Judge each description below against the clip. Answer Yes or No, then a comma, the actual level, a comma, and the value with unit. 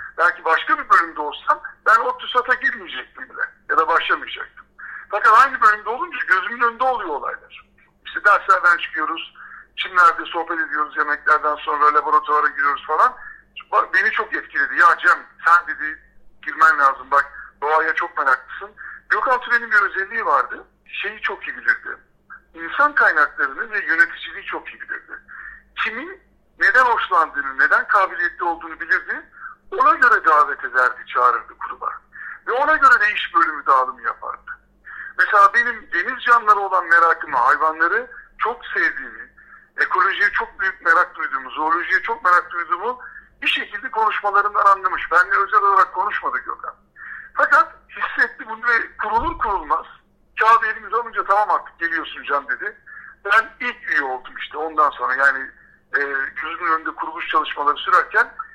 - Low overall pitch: No, high, 225 Hz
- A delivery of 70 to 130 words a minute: No, fast, 140 wpm